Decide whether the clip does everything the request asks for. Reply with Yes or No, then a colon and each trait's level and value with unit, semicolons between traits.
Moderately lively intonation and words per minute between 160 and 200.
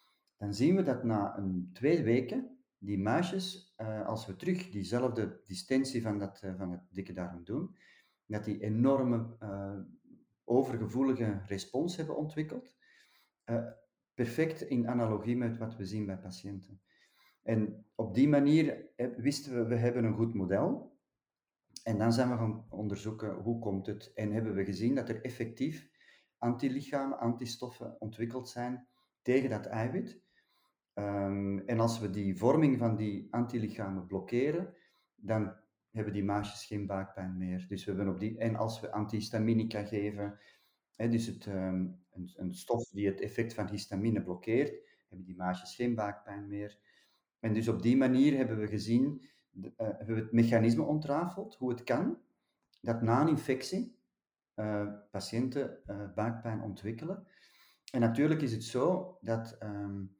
No: average, 3.6 semitones; average, 150 wpm